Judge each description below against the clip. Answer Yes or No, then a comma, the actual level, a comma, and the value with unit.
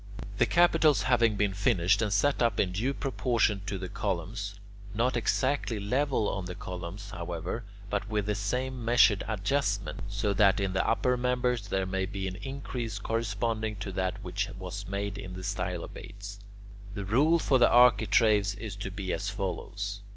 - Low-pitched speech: Yes, low, 105 Hz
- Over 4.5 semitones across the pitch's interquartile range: No, average, 3.5 semitones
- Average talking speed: Yes, average, 170 wpm